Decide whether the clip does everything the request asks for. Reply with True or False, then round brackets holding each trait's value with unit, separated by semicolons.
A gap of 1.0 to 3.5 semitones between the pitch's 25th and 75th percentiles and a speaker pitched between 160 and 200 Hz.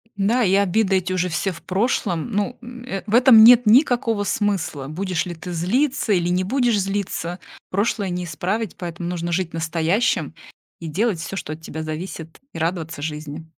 False (4.5 semitones; 185 Hz)